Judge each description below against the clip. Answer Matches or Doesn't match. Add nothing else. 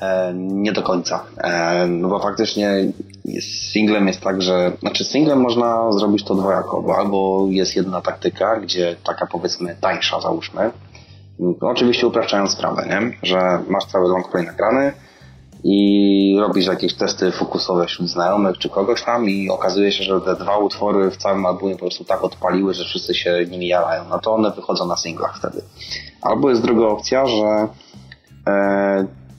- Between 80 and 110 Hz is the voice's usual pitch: Matches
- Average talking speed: Doesn't match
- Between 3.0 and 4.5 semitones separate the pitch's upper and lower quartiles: Doesn't match